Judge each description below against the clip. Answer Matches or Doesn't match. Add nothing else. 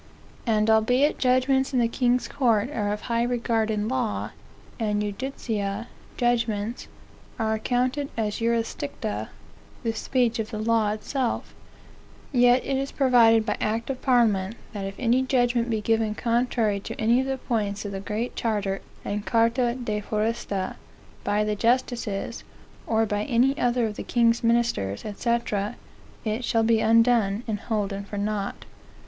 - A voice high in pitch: Matches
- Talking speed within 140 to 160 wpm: Matches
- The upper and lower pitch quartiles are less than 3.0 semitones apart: Matches